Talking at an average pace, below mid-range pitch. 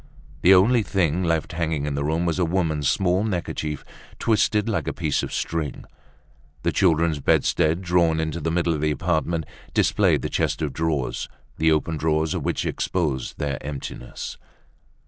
Yes: average, 165 wpm; very low, 80 Hz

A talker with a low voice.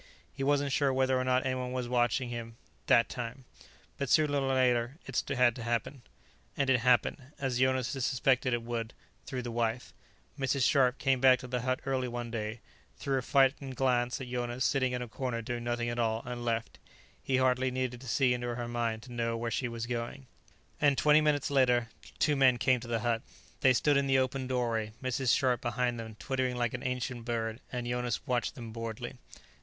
Yes: low, 125 Hz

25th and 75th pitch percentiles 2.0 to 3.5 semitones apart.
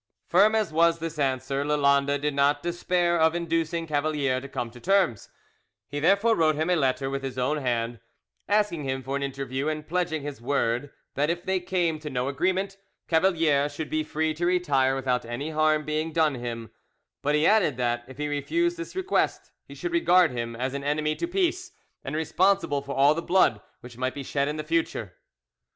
No: average, 4.1 semitones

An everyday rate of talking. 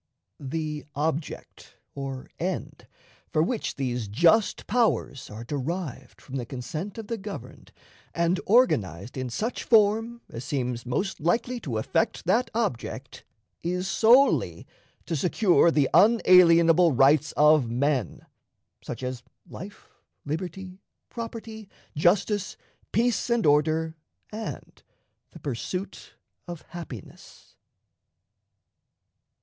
No: slow, 110 wpm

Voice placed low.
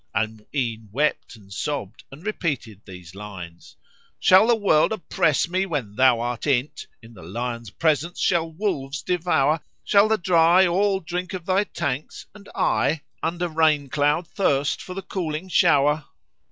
No: medium, 150 Hz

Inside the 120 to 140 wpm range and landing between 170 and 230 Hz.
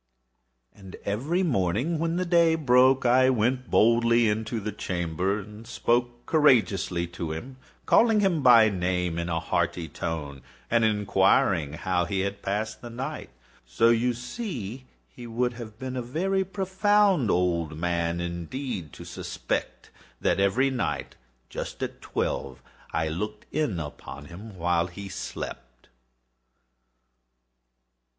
No: slow, 135 wpm; low, 110 Hz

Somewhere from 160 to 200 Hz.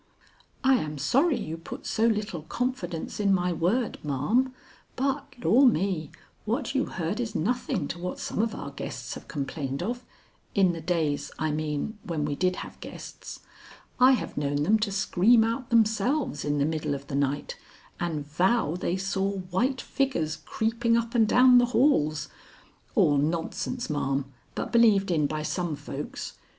Yes: high, 190 Hz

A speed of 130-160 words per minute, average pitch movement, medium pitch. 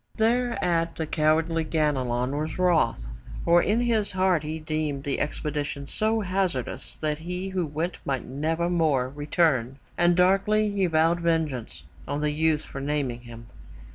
Yes: average, 150 wpm; average, 3.7 semitones; medium, 160 Hz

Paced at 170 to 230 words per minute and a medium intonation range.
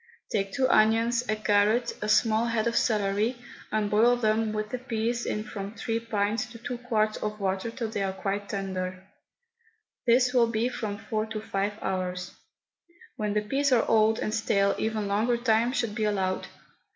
No: average, 175 wpm; narrow, 2.2 semitones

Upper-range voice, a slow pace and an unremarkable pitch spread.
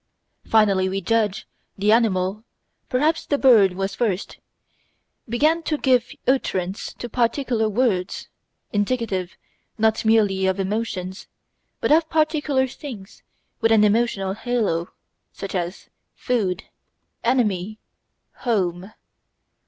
Yes: high, 215 Hz; slow, 105 wpm; average, 4.3 semitones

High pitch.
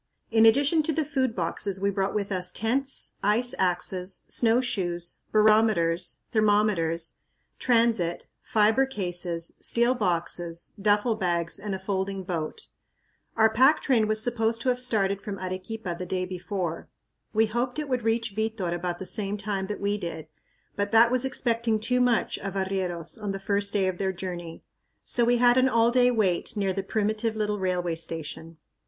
Yes: high, 205 Hz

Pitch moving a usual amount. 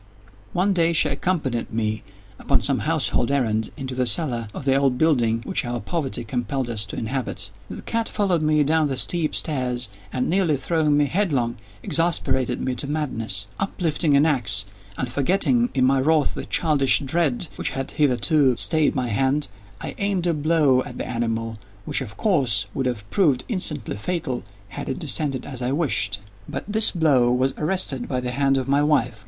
Yes: average, 4.4 semitones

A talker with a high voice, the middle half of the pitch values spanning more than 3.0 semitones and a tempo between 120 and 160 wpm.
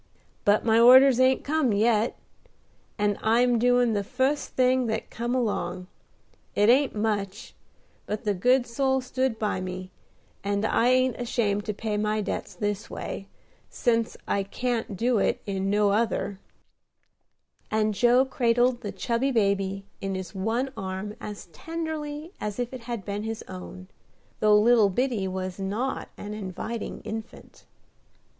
Yes: high, 220 Hz; average, 3.5 semitones; average, 150 wpm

